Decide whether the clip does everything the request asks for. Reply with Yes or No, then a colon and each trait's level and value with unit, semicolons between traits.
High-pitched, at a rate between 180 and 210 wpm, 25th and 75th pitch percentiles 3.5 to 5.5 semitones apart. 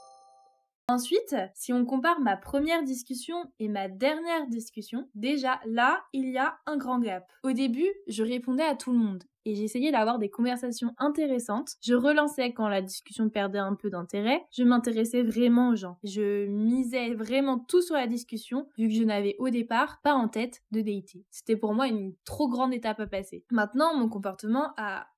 Yes: high, 245 Hz; average, 185 wpm; average, 3.8 semitones